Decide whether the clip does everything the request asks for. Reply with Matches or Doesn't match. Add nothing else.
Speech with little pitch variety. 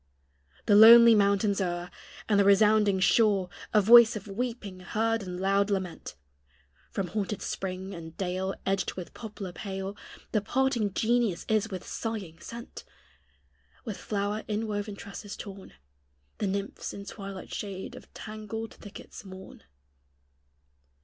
Matches